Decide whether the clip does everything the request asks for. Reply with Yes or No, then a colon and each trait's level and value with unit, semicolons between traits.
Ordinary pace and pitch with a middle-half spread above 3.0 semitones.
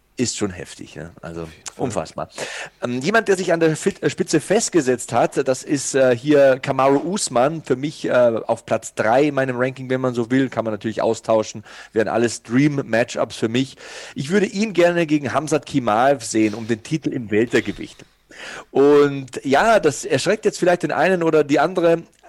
Yes: average, 180 wpm; average, 5.2 semitones